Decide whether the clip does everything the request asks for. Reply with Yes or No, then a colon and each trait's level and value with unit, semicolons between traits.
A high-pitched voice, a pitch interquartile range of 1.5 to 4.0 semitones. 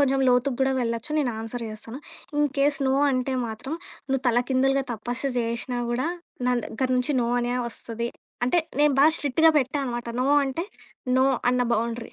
Yes: very high, 250 Hz; narrow, 2.5 semitones